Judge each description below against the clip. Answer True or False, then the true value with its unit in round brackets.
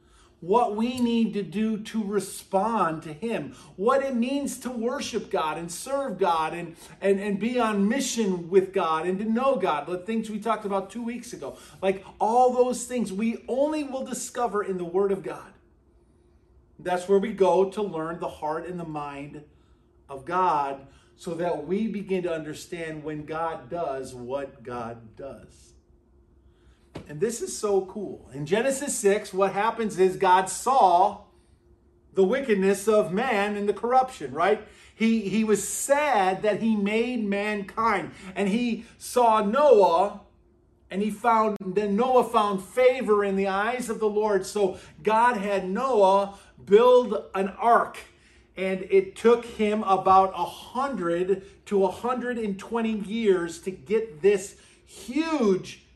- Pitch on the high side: True (200 Hz)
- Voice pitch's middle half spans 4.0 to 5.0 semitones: False (3.6 semitones)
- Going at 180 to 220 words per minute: False (155 wpm)